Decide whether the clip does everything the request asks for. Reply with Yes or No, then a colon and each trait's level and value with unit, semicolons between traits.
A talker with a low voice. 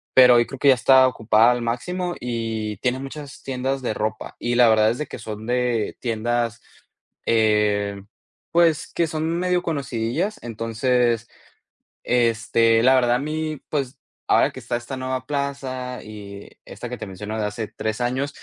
Yes: low, 120 Hz